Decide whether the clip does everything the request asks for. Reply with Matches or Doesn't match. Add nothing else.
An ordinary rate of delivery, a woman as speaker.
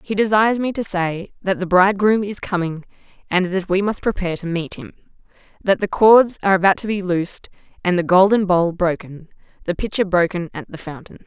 Matches